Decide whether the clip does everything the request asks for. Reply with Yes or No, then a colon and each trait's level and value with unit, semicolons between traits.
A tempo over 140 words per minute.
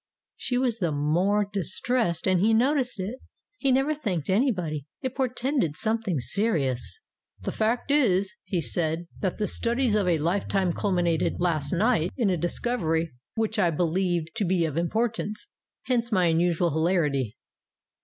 Yes: average, 160 wpm